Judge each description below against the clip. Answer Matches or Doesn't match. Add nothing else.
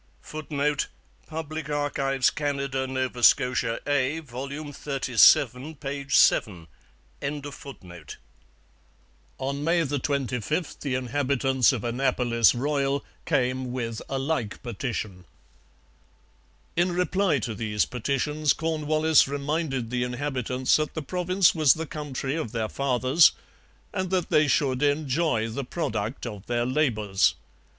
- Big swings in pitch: Doesn't match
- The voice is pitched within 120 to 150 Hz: Matches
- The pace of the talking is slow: Matches